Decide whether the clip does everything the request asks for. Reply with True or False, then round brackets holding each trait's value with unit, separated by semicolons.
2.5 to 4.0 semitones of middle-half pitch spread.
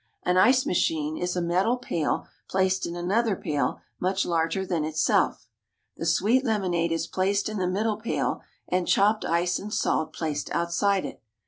True (3.1 semitones)